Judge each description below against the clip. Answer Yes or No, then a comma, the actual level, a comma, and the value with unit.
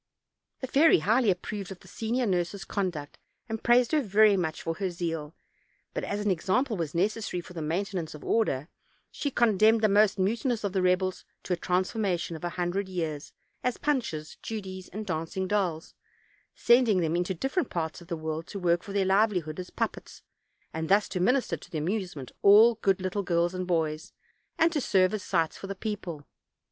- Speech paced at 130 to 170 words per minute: No, average, 195 wpm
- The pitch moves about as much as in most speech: Yes, average, 3.9 semitones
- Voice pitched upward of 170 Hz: Yes, high, 190 Hz